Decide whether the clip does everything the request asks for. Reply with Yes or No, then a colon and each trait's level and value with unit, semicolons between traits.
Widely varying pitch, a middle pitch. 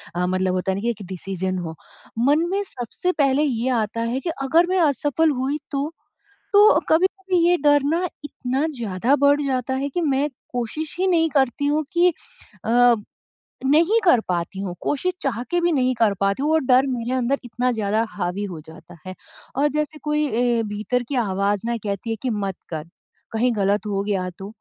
No: wide, 6.5 semitones; very high, 250 Hz